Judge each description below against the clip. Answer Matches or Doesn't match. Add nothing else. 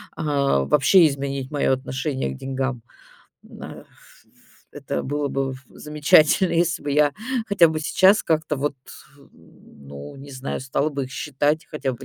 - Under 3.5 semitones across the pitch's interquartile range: Matches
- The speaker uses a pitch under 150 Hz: Matches